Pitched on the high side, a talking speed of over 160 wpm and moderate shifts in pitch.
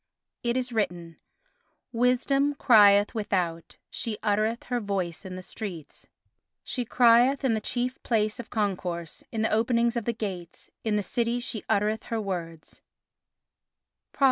No: high, 220 Hz; average, 145 wpm; average, 3.6 semitones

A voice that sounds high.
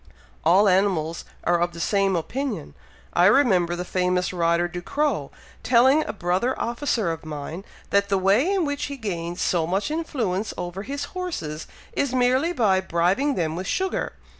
Yes: high, 195 Hz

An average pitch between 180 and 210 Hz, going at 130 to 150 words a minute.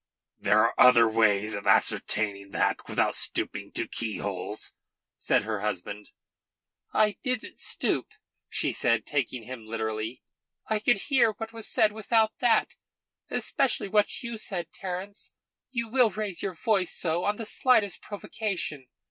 Yes: medium, 185 Hz; average, 140 wpm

